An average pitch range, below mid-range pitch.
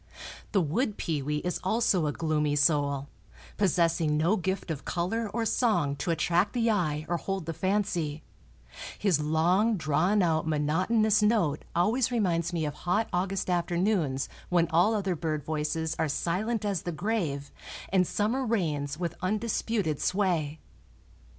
No: average, 4.9 semitones; medium, 175 Hz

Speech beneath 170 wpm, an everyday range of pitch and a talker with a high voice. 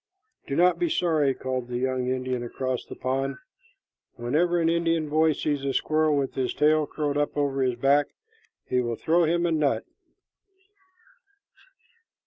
No: average, 155 wpm; average, 3.5 semitones; medium, 145 Hz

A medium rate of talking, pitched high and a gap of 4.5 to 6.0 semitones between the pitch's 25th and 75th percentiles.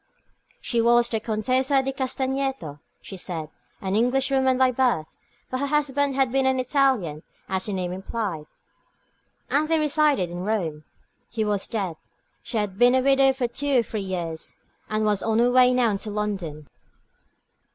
Yes: average, 165 wpm; high, 235 Hz; wide, 5.5 semitones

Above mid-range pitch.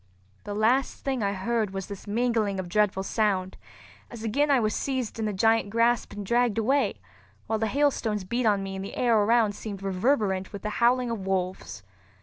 Yes: high, 215 Hz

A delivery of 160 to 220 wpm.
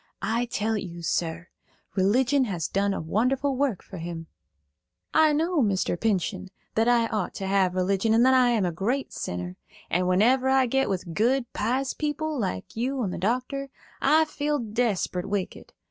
Yes: average, 175 wpm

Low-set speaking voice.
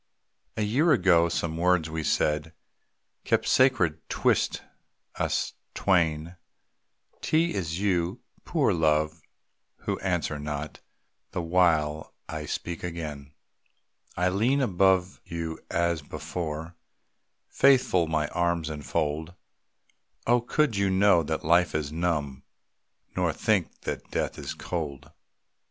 Yes: very low, 85 Hz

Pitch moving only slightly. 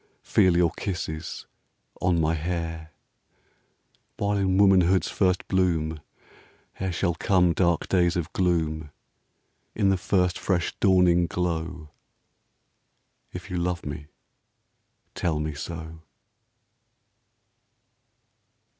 Yes: narrow, 2.2 semitones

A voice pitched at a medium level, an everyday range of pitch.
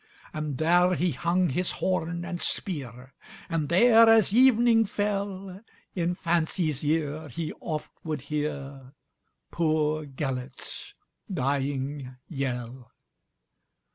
Yes: medium, 155 Hz; average, 4.7 semitones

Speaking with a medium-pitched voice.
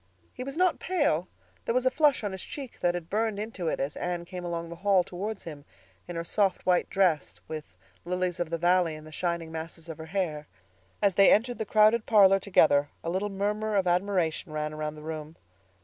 Yes: medium, 180 Hz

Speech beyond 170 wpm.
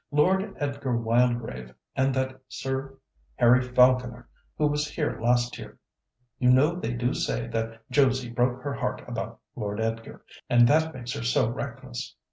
No: average, 155 wpm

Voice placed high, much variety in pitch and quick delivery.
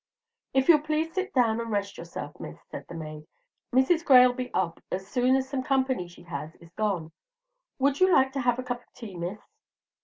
Yes: high, 245 Hz; wide, 6.2 semitones; fast, 210 wpm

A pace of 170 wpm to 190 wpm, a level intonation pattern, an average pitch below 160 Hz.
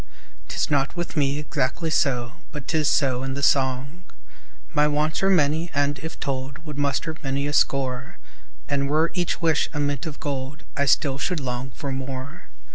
Yes: average, 180 wpm; narrow, 2.3 semitones; medium, 140 Hz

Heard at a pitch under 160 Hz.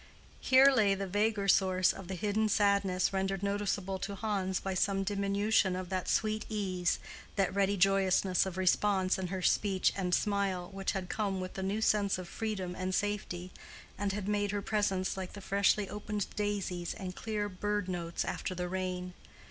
No: high, 195 Hz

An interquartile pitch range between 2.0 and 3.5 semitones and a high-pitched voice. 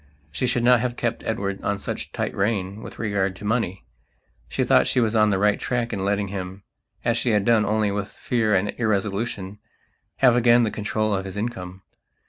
No: average, 2.9 semitones; low, 105 Hz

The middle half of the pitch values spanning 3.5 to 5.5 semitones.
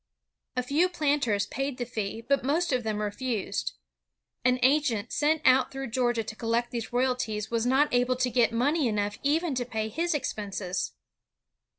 Yes: average, 3.8 semitones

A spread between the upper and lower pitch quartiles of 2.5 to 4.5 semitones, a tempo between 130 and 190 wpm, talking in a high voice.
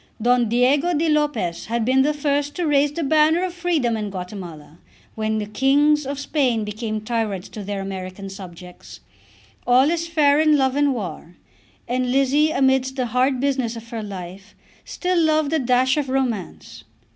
No: wide, 5.4 semitones; average, 170 wpm; very high, 255 Hz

